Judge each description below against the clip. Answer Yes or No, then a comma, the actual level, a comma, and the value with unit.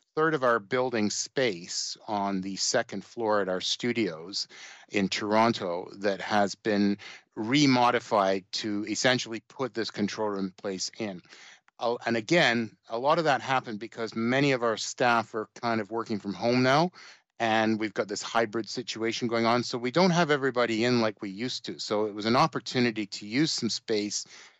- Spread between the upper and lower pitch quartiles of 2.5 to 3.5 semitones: Yes, average, 2.8 semitones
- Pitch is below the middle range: Yes, low, 115 Hz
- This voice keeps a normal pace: Yes, average, 175 wpm